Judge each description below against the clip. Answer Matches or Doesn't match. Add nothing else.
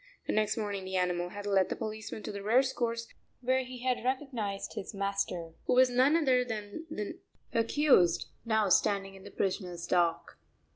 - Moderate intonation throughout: Matches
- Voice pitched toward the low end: Doesn't match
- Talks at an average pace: Matches